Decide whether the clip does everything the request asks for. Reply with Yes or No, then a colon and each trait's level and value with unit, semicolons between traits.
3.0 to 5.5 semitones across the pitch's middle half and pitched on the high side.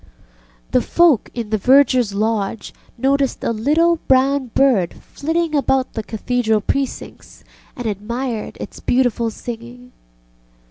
Yes: average, 3.7 semitones; high, 245 Hz